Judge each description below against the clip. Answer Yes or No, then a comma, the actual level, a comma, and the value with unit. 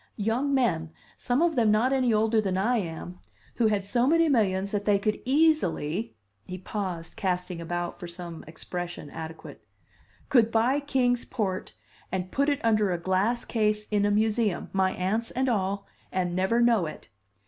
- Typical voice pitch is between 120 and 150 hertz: No, high, 205 Hz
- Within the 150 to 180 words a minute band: Yes, average, 175 wpm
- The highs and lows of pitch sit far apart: No, average, 4.7 semitones